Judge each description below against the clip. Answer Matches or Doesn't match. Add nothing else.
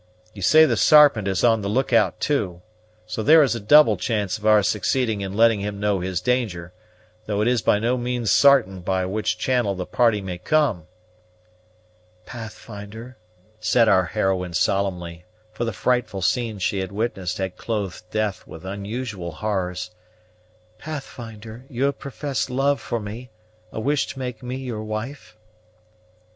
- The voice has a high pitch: Doesn't match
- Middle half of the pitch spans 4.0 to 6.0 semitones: Matches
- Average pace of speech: Matches